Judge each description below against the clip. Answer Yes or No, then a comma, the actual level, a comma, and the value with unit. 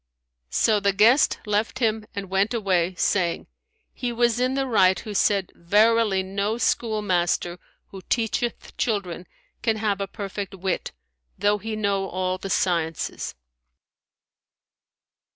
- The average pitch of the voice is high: Yes, high, 200 Hz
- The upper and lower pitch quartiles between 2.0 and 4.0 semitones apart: Yes, average, 2.8 semitones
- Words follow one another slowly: Yes, slow, 130 wpm